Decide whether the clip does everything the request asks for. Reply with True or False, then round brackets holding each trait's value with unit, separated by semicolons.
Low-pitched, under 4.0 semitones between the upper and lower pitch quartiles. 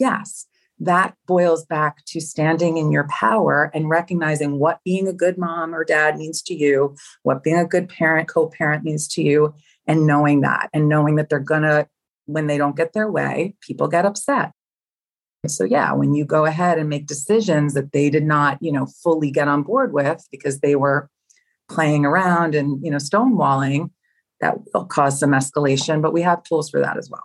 False (155 Hz; 2.4 semitones)